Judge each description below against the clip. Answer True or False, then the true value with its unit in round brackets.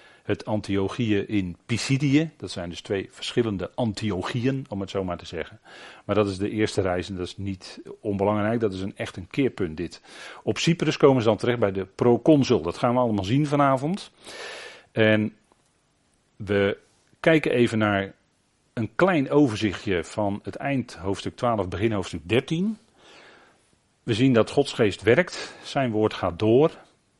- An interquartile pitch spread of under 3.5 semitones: False (4.9 semitones)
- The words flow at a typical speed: True (165 wpm)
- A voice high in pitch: False (110 Hz)